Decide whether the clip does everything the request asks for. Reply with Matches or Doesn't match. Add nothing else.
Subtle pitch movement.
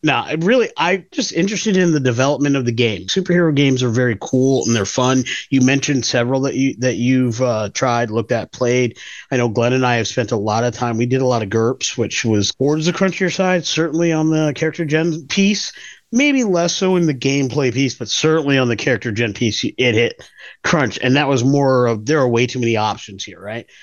Doesn't match